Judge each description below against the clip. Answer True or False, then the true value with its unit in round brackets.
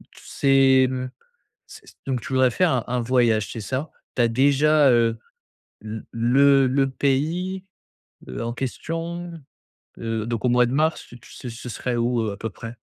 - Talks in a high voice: False (130 Hz)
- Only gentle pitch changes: False (3.1 semitones)